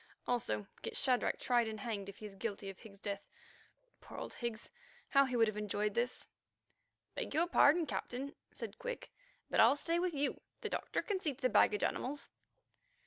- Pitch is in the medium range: No, high, 240 Hz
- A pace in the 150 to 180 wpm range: No, average, 190 wpm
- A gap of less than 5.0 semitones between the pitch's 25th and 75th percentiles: No, wide, 5.4 semitones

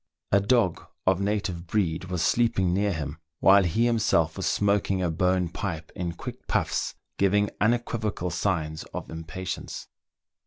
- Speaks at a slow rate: No, average, 150 wpm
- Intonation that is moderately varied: Yes, average, 3.2 semitones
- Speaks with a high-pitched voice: No, very low, 95 Hz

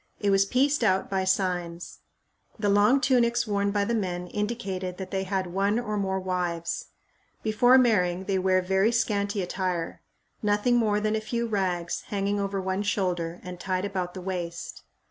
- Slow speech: No, average, 170 wpm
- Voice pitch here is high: Yes, high, 195 Hz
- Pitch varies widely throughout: No, narrow, 2.5 semitones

